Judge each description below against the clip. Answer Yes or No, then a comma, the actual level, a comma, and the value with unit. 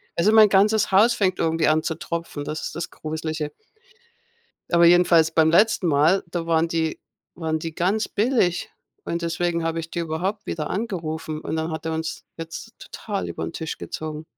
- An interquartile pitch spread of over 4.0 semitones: No, average, 2.8 semitones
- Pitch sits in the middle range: Yes, medium, 165 Hz